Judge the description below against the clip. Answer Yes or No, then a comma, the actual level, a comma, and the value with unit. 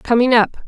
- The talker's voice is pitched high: Yes, high, 235 Hz